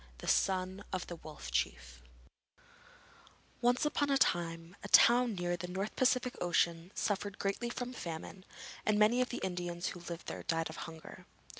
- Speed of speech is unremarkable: Yes, average, 165 wpm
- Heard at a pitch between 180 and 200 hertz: Yes, medium, 185 Hz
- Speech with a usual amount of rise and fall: No, wide, 5.7 semitones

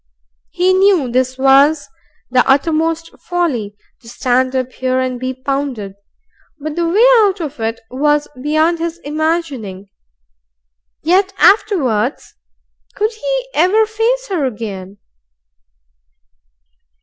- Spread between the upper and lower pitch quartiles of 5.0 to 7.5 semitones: Yes, wide, 5.6 semitones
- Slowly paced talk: Yes, slow, 115 wpm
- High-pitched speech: Yes, very high, 295 Hz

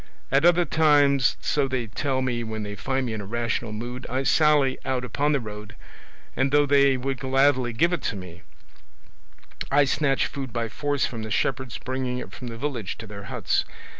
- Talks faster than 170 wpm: Yes, average, 195 wpm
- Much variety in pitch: No, average, 3.5 semitones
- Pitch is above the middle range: No, low, 130 Hz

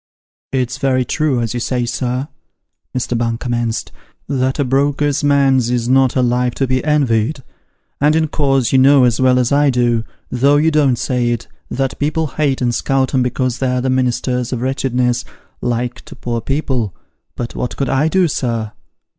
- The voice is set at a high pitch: No, low, 130 Hz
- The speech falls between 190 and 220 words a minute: No, average, 180 wpm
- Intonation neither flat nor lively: No, narrow, 2.1 semitones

